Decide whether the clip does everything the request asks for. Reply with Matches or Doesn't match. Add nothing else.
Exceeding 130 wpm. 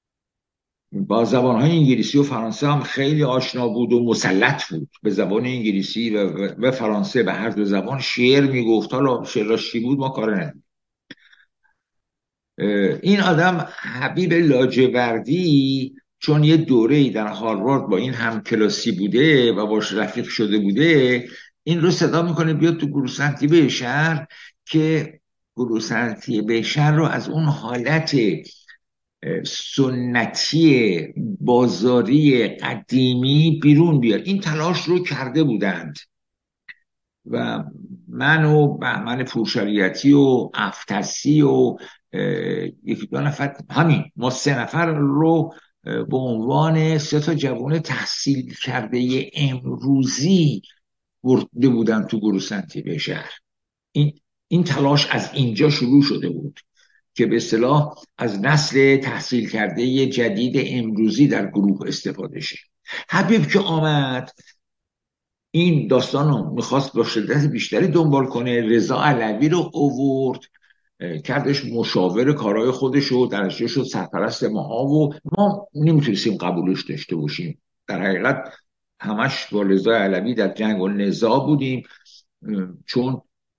Doesn't match